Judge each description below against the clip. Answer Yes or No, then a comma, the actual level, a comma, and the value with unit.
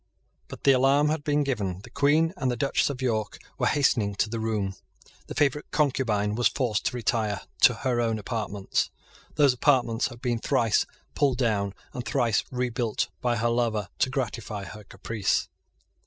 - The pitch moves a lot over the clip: No, average, 3.9 semitones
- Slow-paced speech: No, average, 170 wpm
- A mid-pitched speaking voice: No, low, 120 Hz